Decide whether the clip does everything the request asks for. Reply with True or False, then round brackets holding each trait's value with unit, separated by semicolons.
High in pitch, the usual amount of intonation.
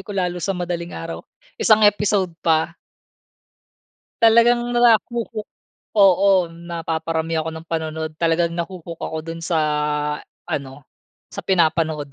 False (170 Hz; 3.4 semitones)